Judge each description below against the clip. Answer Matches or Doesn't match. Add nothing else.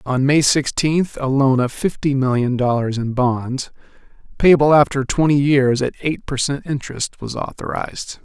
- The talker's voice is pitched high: Doesn't match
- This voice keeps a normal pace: Matches